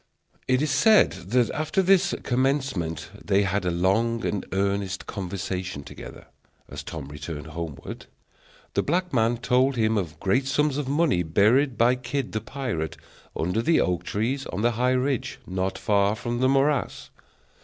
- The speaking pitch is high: No, low, 115 Hz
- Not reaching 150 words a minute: No, average, 160 wpm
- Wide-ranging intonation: Yes, wide, 6.2 semitones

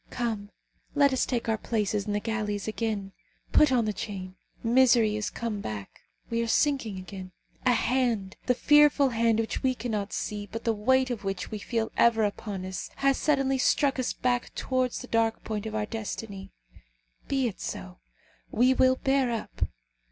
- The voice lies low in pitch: No, high, 225 Hz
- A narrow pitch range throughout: No, average, 3.5 semitones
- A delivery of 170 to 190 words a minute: Yes, average, 180 wpm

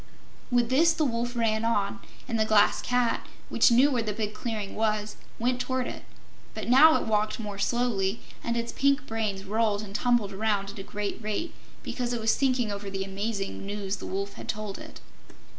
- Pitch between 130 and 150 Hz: No, high, 220 Hz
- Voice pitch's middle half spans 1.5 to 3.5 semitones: Yes, average, 3.0 semitones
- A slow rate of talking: No, average, 195 wpm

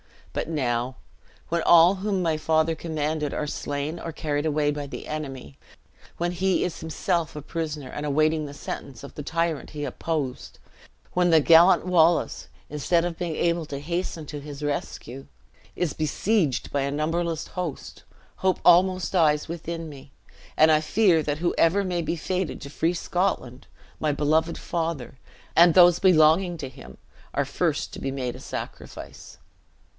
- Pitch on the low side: No, medium, 160 Hz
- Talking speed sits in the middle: Yes, average, 160 wpm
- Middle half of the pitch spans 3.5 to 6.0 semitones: No, average, 2.8 semitones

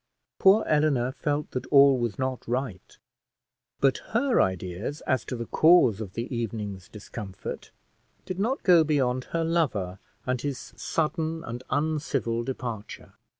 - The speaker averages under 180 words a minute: Yes, average, 140 wpm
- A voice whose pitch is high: No, low, 130 Hz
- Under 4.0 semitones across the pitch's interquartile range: No, average, 5.1 semitones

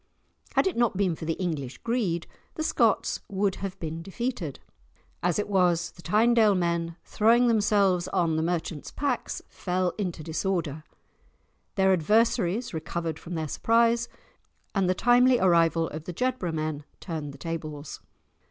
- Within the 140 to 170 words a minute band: Yes, average, 150 wpm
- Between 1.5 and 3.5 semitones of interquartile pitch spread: No, average, 4.6 semitones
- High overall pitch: No, medium, 180 Hz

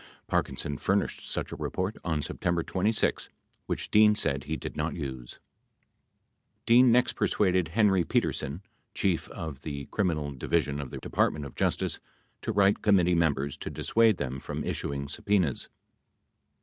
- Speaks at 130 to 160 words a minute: Yes, average, 150 wpm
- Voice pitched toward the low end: Yes, very low, 85 Hz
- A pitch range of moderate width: No, wide, 5.8 semitones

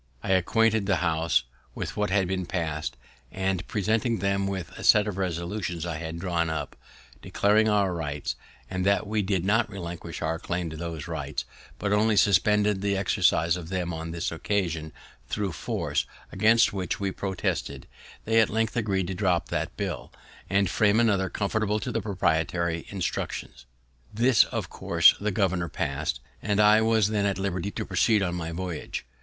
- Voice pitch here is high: No, very low, 95 Hz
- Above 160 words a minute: Yes, average, 170 wpm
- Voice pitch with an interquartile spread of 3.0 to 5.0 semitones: Yes, average, 3.4 semitones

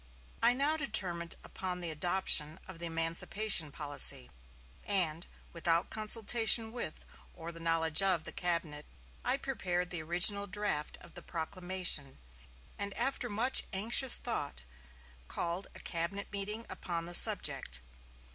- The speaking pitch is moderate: Yes, medium, 180 Hz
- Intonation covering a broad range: No, average, 4.0 semitones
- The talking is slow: Yes, slow, 130 wpm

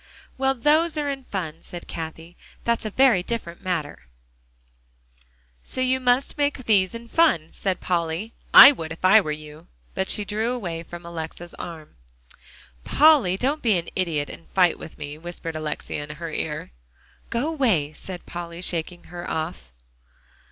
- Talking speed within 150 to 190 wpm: Yes, average, 160 wpm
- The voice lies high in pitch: No, medium, 180 Hz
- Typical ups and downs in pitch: No, wide, 6.4 semitones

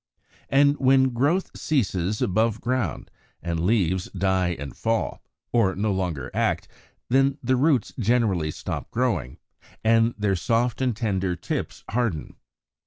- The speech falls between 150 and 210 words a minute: No, slow, 135 wpm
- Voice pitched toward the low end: Yes, low, 110 Hz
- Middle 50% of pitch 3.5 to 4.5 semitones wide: No, average, 5.1 semitones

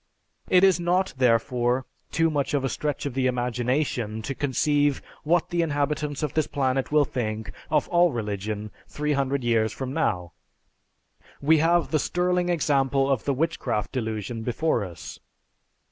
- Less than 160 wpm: Yes, average, 150 wpm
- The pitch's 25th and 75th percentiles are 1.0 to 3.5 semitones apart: No, average, 4.3 semitones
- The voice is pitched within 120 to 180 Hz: Yes, medium, 140 Hz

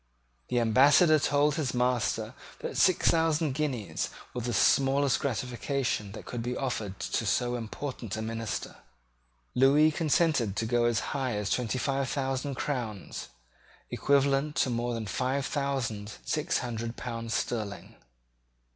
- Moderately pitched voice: No, low, 125 Hz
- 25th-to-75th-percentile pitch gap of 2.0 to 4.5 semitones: Yes, average, 3.4 semitones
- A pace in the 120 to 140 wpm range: Yes, slow, 135 wpm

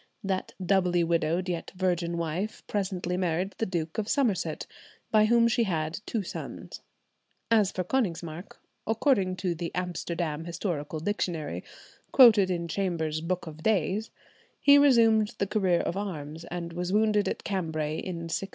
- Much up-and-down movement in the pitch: No, average, 3.6 semitones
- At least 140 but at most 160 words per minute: Yes, average, 150 wpm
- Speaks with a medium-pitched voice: Yes, medium, 180 Hz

